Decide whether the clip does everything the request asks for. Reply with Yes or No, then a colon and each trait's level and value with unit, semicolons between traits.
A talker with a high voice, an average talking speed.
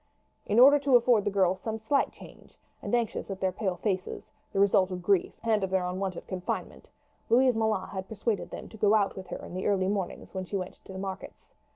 No: high, 195 Hz; fast, 225 wpm